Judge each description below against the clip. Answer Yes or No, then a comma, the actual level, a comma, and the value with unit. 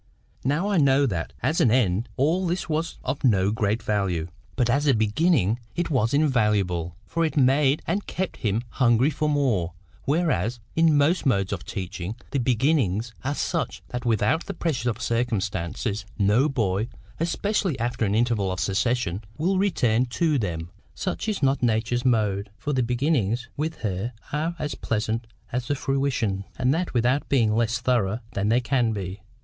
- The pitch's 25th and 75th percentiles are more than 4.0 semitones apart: Yes, average, 5.3 semitones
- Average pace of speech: Yes, average, 170 wpm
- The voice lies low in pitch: Yes, low, 120 Hz